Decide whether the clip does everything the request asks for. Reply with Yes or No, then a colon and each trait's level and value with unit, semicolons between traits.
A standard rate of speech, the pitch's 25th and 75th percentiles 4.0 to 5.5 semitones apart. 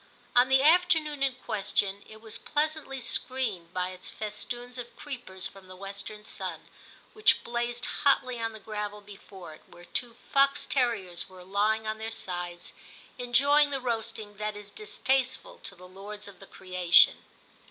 Yes: average, 160 wpm; average, 4.7 semitones